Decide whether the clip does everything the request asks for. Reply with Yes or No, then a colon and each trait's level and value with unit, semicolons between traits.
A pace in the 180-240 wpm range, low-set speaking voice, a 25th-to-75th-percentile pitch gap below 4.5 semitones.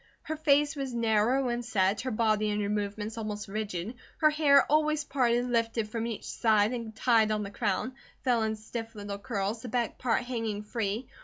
No: average, 190 wpm; high, 225 Hz; average, 3.0 semitones